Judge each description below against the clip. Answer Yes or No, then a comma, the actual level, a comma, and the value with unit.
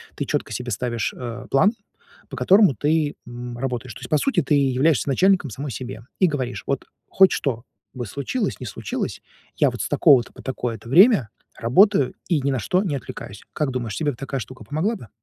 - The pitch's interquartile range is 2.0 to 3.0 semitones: No, average, 4.7 semitones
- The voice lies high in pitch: No, low, 135 Hz